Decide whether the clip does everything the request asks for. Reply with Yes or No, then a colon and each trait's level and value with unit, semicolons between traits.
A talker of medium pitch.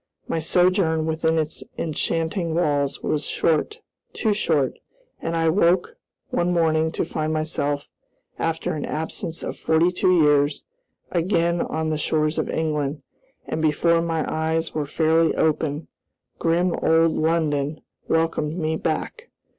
Yes: medium, 160 Hz